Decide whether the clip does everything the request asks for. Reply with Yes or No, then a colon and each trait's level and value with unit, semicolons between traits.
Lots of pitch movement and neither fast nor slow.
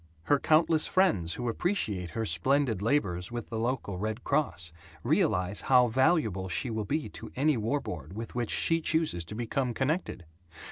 Yes: wide, 6.8 semitones; average, 170 wpm